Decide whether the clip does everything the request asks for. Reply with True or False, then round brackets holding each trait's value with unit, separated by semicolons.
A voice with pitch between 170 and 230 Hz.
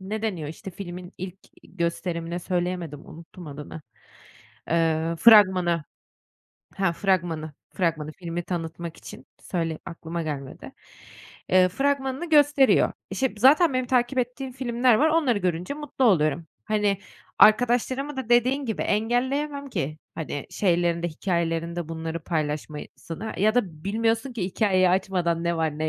True (185 Hz)